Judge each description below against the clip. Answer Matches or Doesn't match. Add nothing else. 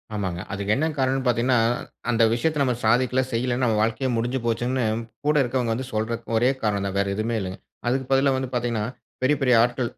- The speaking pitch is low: Matches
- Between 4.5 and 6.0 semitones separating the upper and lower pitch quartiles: Doesn't match